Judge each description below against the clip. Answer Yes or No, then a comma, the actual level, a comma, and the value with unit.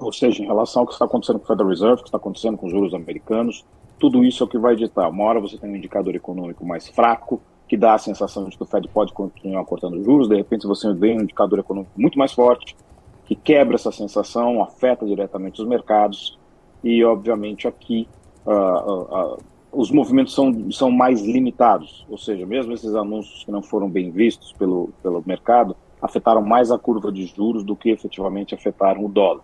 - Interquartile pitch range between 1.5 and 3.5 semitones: Yes, average, 3.2 semitones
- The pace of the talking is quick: Yes, fast, 210 wpm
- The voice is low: Yes, low, 105 Hz